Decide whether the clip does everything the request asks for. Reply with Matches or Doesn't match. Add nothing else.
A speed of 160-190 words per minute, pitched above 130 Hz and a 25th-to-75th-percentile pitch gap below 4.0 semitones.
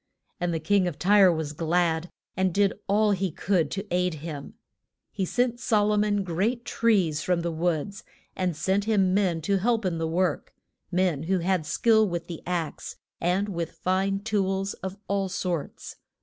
Matches